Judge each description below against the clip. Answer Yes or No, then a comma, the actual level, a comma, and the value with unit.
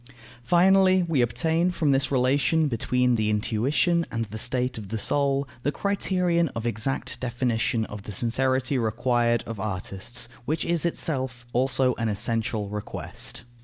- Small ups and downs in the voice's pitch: No, average, 4.4 semitones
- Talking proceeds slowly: No, average, 145 wpm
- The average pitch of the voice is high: No, low, 125 Hz